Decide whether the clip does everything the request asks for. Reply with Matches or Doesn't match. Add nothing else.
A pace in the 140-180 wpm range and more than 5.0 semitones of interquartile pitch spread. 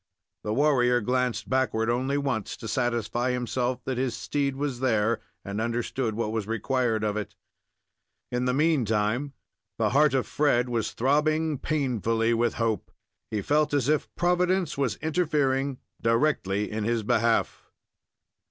Doesn't match